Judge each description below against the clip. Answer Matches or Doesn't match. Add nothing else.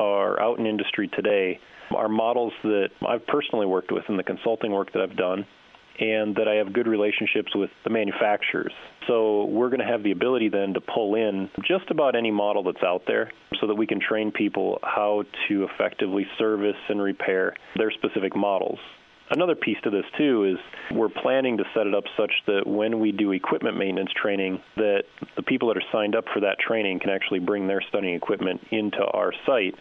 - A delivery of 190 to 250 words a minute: Matches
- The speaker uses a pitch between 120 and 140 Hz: Doesn't match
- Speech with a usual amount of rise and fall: Doesn't match